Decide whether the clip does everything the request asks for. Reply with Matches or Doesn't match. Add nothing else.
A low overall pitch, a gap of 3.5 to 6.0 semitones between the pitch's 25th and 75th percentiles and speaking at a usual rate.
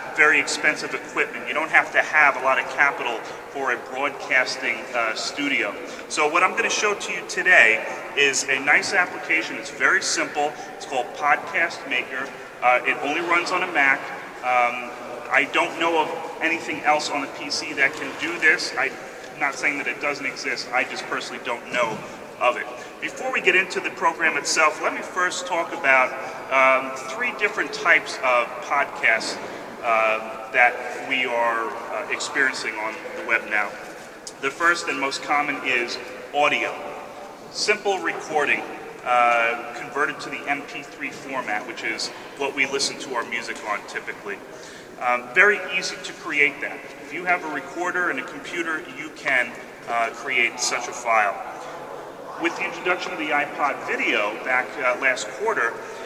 Matches